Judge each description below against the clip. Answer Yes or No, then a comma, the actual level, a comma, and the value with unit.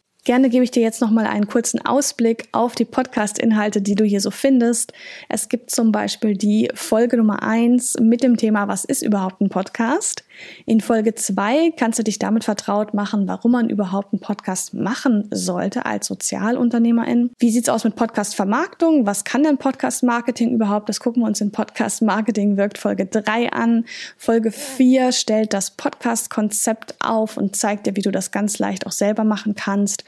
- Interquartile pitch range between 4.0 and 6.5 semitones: No, narrow, 2.6 semitones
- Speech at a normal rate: Yes, average, 180 wpm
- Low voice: No, high, 225 Hz